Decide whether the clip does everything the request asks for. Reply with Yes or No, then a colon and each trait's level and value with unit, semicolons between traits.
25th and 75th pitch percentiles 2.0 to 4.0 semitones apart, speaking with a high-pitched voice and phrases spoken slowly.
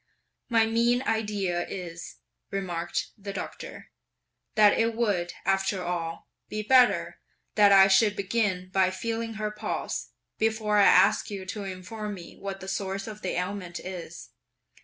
No: narrow, 2.6 semitones; high, 200 Hz; average, 145 wpm